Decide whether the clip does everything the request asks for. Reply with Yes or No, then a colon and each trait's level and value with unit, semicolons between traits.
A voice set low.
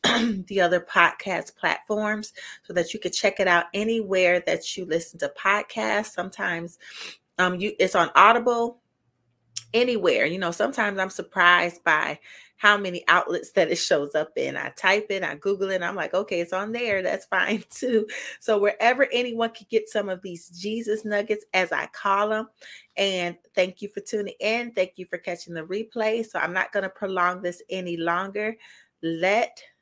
No: high, 195 Hz